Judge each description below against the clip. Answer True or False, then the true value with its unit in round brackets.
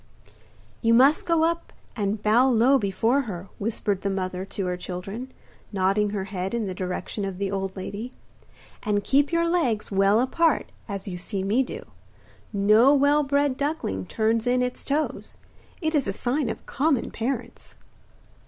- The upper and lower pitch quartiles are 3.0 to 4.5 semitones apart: False (5.6 semitones)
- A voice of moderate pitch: False (225 Hz)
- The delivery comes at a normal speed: True (165 wpm)